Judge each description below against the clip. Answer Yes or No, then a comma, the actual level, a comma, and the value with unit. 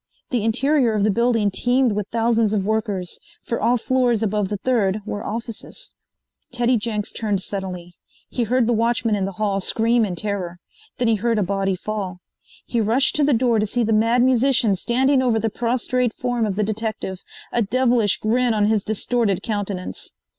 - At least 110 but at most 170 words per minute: No, average, 185 wpm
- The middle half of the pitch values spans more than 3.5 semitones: No, average, 2.9 semitones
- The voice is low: No, high, 220 Hz